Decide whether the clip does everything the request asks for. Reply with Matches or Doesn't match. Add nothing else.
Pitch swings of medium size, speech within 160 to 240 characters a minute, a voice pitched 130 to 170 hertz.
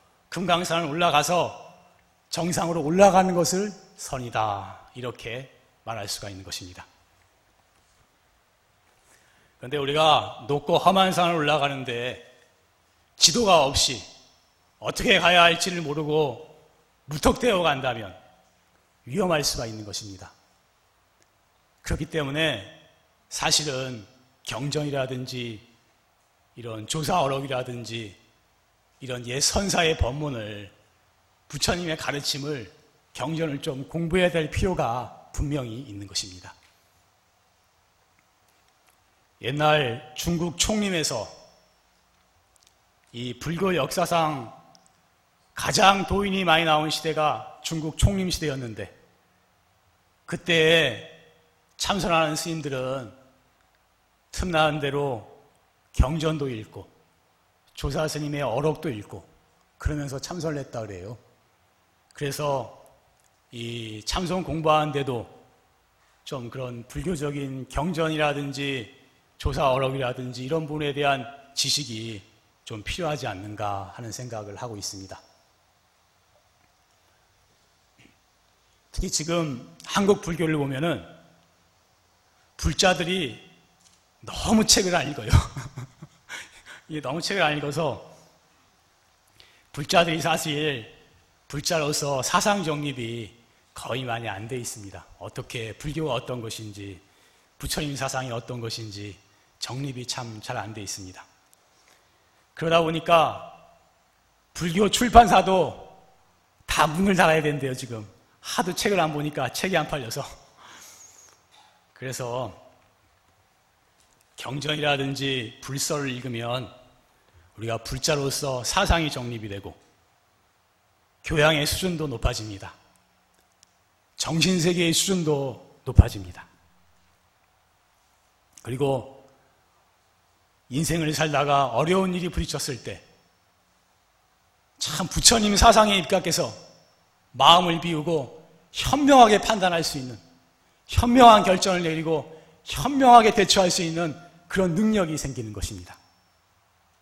Doesn't match